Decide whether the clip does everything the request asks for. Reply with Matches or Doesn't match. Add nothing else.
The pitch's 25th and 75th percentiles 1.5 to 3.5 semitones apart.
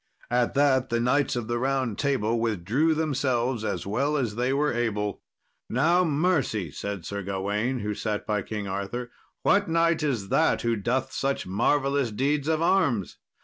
Doesn't match